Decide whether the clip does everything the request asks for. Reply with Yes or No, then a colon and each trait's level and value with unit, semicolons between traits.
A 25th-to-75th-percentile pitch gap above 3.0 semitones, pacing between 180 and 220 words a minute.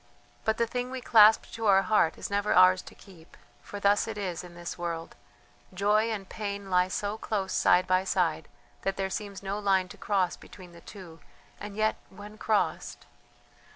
No: narrow, 2.4 semitones; average, 190 wpm